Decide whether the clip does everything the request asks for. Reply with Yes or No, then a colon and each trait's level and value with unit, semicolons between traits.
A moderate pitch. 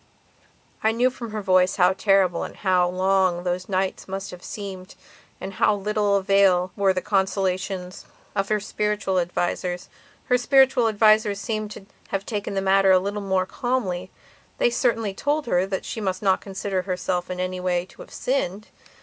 No: high, 195 Hz